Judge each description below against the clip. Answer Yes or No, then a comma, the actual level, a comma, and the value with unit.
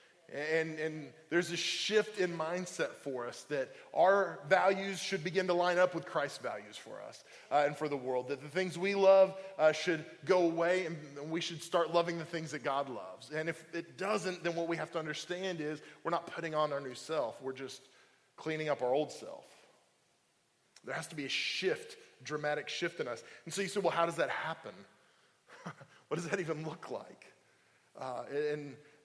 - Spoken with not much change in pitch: No, average, 3.3 semitones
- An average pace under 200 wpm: No, fast, 205 wpm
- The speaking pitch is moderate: Yes, medium, 165 Hz